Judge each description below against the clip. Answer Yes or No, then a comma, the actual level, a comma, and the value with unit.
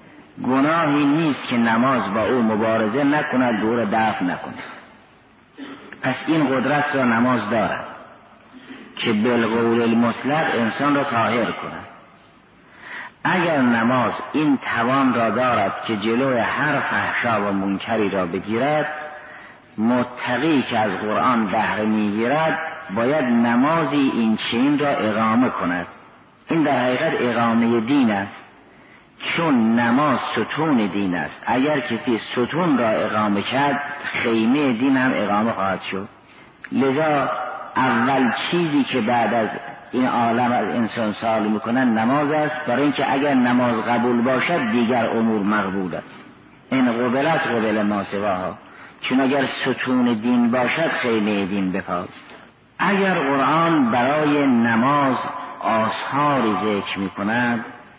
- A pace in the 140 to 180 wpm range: No, average, 120 wpm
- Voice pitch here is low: Yes, low, 120 Hz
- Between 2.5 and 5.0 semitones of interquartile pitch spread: Yes, average, 3.8 semitones